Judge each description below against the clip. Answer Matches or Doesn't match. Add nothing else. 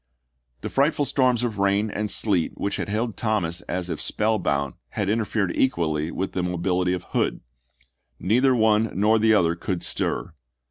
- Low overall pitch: Matches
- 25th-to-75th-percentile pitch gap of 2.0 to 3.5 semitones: Doesn't match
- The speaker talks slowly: Doesn't match